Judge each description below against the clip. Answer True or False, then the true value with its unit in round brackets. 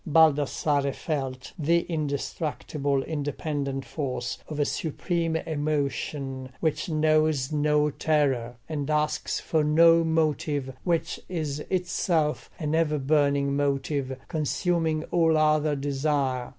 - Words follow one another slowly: True (110 wpm)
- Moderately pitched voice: True (150 Hz)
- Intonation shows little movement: True (2.2 semitones)